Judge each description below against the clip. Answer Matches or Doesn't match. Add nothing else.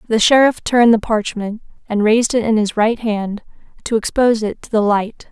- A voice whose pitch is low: Doesn't match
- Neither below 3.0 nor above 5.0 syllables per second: Doesn't match